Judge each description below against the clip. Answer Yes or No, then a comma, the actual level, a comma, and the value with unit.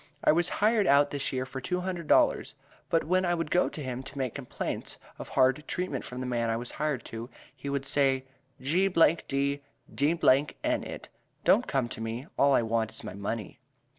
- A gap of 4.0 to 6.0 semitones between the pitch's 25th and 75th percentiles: Yes, average, 4.7 semitones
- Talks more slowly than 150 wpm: No, fast, 205 wpm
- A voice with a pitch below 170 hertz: Yes, medium, 140 Hz